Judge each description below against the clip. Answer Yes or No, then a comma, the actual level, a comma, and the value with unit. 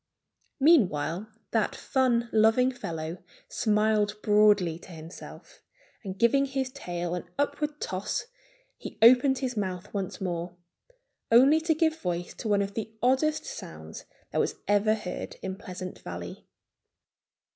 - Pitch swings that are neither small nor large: No, wide, 6.0 semitones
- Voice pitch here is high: Yes, high, 210 Hz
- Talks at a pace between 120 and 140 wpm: Yes, slow, 135 wpm